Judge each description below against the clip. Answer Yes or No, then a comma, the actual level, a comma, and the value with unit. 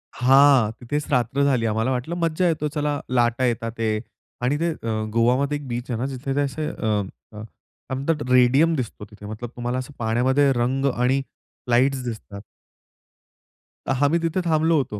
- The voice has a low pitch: Yes, low, 130 Hz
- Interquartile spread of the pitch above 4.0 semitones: No, average, 3.3 semitones